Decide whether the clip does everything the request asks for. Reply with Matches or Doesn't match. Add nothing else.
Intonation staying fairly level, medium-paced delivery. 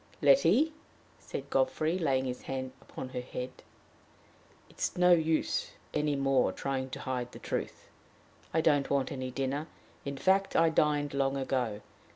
Doesn't match